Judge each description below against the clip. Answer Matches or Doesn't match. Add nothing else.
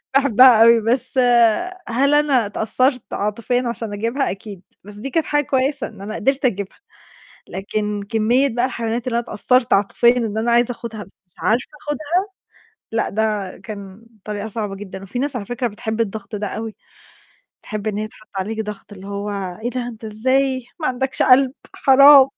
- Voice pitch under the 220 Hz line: Doesn't match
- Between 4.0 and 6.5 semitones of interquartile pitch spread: Doesn't match